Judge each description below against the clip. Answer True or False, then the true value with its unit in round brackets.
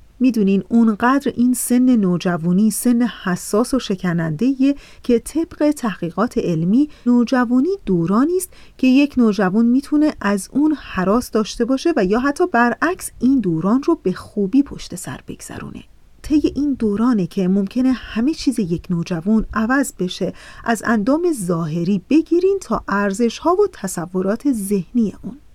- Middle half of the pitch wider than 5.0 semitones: True (5.5 semitones)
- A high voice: True (235 Hz)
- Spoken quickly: False (140 wpm)